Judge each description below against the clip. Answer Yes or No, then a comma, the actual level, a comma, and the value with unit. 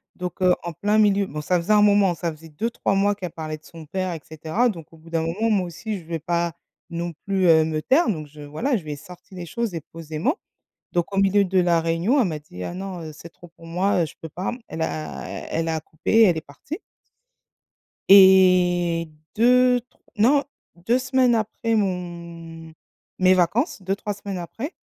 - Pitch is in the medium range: Yes, medium, 180 Hz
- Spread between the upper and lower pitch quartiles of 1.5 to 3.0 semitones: No, average, 3.8 semitones